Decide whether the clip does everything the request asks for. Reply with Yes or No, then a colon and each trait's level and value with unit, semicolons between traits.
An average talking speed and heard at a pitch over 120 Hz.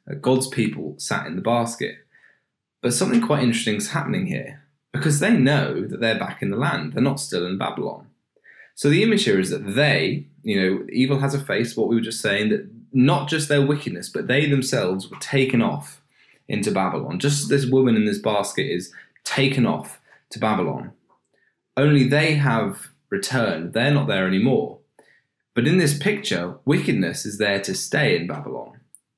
Yes: average, 180 wpm; medium, 140 Hz